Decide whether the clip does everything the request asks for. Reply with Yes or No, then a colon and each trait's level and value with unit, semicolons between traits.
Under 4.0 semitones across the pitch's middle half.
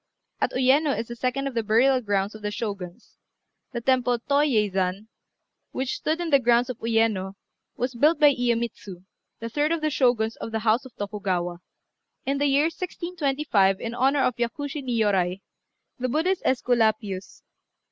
No: average, 4.6 semitones